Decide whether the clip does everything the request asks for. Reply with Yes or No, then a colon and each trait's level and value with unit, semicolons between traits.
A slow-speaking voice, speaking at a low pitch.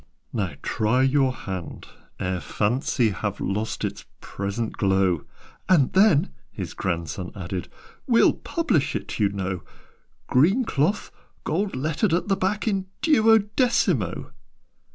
Yes: slow, 125 wpm; low, 130 Hz